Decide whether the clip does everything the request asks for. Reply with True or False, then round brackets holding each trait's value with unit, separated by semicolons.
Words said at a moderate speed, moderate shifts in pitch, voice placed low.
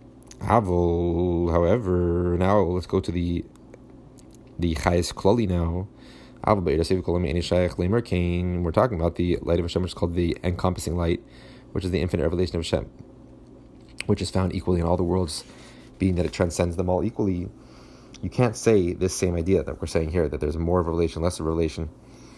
False (175 wpm; 1.6 semitones; 90 Hz)